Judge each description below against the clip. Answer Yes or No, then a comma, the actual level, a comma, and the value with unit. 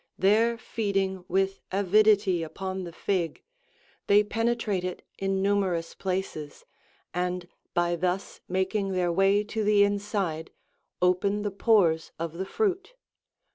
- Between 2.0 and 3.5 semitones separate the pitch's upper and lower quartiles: Yes, narrow, 2.5 semitones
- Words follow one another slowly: Yes, slow, 125 wpm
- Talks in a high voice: Yes, high, 195 Hz